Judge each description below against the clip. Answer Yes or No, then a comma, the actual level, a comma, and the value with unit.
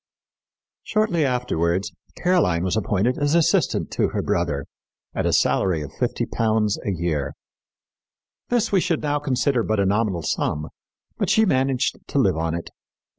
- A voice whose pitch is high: No, low, 110 Hz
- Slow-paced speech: No, average, 150 wpm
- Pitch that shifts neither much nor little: No, wide, 9.0 semitones